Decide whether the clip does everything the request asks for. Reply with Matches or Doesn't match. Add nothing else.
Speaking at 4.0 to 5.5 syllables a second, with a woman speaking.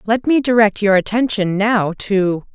Matches